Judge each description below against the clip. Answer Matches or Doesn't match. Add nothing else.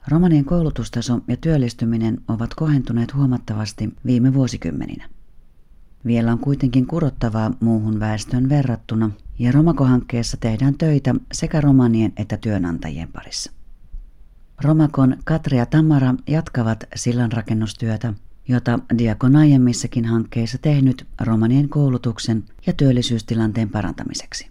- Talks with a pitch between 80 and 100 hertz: Doesn't match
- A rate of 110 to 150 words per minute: Doesn't match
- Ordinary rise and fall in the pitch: Matches